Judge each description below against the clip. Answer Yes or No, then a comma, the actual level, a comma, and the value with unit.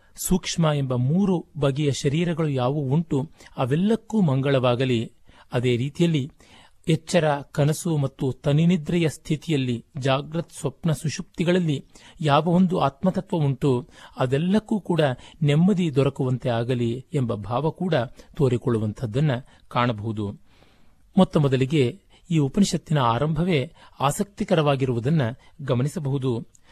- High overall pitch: No, medium, 145 Hz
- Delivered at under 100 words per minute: Yes, average, 90 wpm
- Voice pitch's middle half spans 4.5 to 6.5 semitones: Yes, average, 4.9 semitones